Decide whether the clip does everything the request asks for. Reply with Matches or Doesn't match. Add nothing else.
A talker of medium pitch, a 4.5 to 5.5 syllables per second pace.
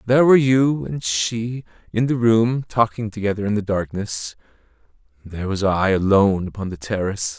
Doesn't match